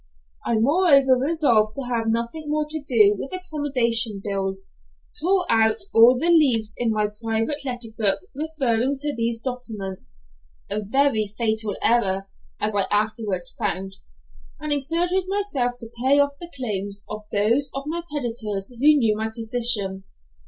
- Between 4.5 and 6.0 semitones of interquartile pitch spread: Yes, average, 5.0 semitones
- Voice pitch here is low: No, high, 235 Hz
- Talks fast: No, average, 150 wpm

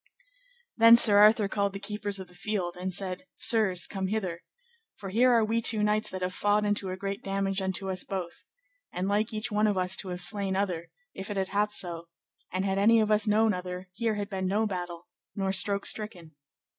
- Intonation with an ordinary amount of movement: No, narrow, 2.3 semitones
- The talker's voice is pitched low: No, high, 200 Hz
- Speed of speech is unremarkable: No, fast, 215 wpm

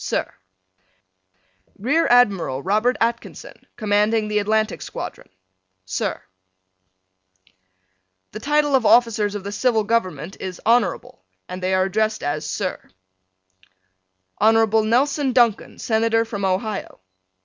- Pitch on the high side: Yes, high, 215 Hz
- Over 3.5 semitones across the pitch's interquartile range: No, average, 3.0 semitones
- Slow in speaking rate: Yes, slow, 110 wpm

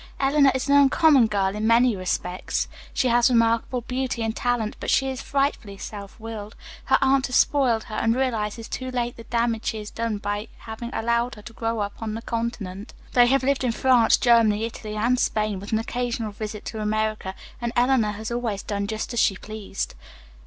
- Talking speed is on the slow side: No, average, 200 wpm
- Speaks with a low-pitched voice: No, high, 230 Hz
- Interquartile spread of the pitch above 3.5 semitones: No, narrow, 2.6 semitones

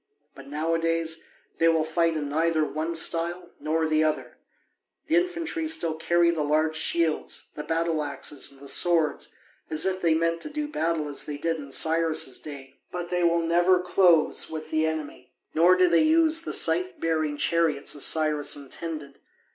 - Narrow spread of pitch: Yes, narrow, 2.0 semitones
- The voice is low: No, medium, 165 Hz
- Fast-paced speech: No, average, 175 wpm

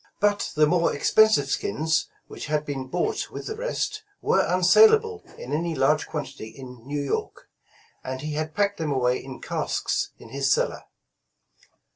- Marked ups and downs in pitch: Yes, wide, 6.7 semitones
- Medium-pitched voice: Yes, medium, 155 Hz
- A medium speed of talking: Yes, average, 160 wpm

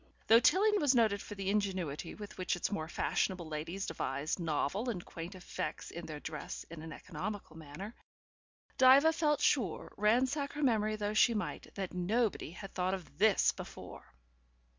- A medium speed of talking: Yes, average, 165 wpm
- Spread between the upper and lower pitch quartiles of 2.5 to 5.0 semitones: No, wide, 5.5 semitones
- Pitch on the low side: No, high, 195 Hz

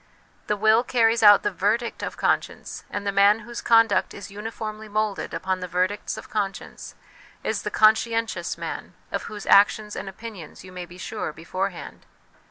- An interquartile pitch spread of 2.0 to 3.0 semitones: Yes, narrow, 2.4 semitones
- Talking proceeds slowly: No, average, 170 wpm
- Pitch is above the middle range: Yes, high, 205 Hz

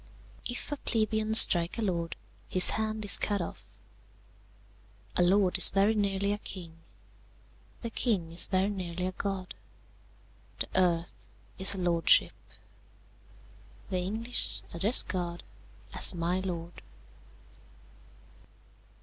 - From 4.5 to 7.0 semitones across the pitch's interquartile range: No, average, 3.1 semitones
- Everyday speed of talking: No, slow, 115 wpm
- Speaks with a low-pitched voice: No, high, 190 Hz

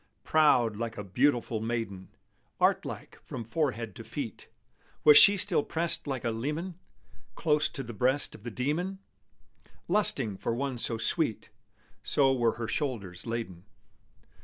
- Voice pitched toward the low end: Yes, low, 120 Hz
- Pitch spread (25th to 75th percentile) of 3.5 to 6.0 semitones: Yes, average, 4.8 semitones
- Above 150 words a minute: No, average, 145 wpm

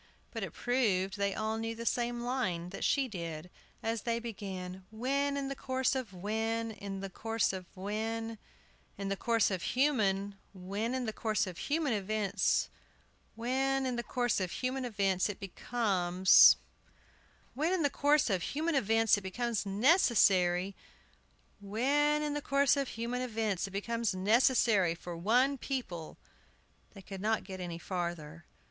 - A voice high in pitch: Yes, high, 220 Hz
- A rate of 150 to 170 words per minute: Yes, average, 160 wpm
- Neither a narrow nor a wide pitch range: Yes, average, 4.6 semitones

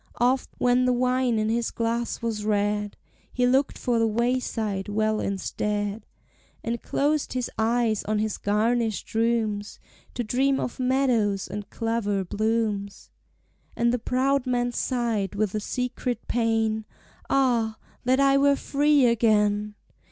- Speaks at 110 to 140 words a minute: Yes, slow, 135 wpm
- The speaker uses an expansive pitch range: No, average, 2.9 semitones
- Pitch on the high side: Yes, high, 230 Hz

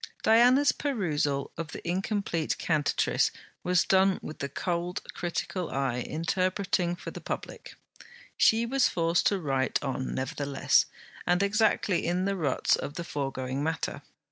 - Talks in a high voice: No, medium, 175 Hz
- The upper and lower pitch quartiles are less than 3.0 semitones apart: No, average, 5.2 semitones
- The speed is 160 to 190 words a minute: No, average, 140 wpm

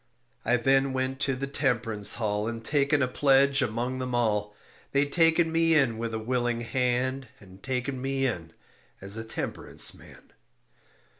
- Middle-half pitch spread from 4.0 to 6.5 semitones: No, average, 3.1 semitones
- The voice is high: No, low, 125 Hz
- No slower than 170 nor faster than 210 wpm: No, average, 160 wpm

